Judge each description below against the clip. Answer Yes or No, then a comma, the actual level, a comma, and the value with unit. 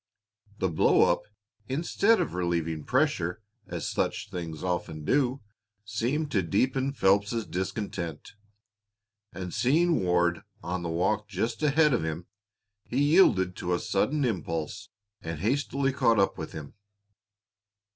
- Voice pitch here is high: No, low, 100 Hz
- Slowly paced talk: Yes, slow, 130 wpm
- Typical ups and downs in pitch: No, wide, 7.3 semitones